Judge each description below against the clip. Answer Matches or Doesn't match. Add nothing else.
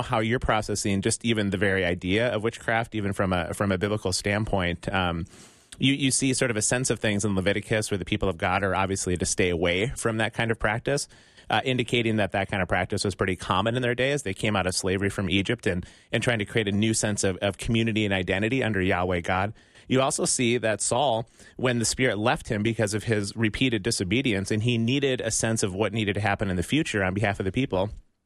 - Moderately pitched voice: Doesn't match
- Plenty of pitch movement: Doesn't match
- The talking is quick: Matches